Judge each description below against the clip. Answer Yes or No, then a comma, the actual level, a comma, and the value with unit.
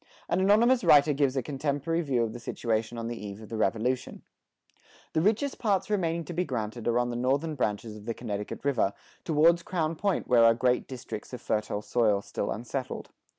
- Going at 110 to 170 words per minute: No, average, 195 wpm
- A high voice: No, low, 125 Hz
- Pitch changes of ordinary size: No, wide, 6.3 semitones